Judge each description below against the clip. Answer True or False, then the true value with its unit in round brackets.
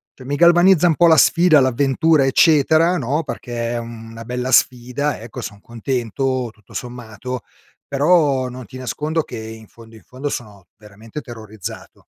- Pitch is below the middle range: True (130 Hz)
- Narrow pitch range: False (4.4 semitones)